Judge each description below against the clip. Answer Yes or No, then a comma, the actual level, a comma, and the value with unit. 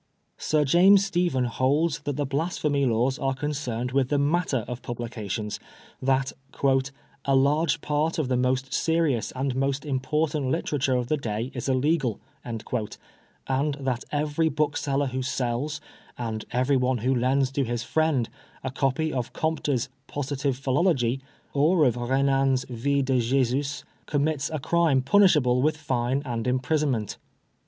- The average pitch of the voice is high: No, low, 135 Hz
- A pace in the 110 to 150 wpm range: Yes, average, 145 wpm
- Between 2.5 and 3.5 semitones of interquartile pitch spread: Yes, average, 2.8 semitones